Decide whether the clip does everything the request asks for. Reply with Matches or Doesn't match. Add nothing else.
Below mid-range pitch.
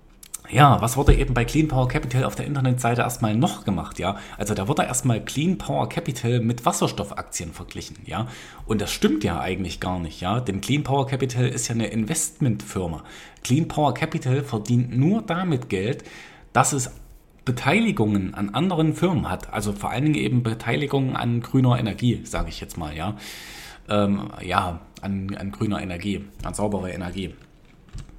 Matches